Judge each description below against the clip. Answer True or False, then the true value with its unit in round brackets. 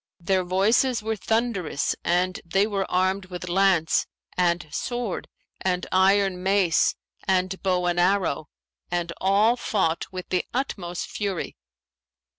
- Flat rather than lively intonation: True (2.1 semitones)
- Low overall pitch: False (185 Hz)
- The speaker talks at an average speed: False (125 wpm)